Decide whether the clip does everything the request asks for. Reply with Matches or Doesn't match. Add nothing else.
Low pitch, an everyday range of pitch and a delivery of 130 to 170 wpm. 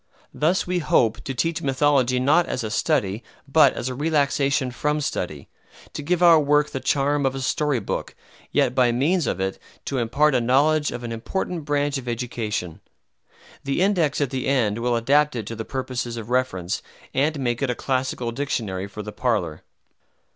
Doesn't match